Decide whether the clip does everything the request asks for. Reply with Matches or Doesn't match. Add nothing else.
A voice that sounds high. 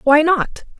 Matches